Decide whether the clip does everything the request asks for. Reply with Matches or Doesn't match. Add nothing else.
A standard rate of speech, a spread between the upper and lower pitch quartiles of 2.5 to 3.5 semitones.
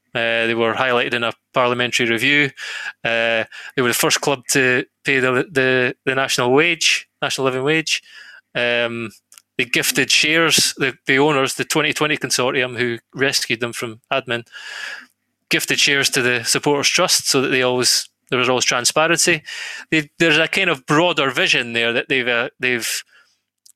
Matches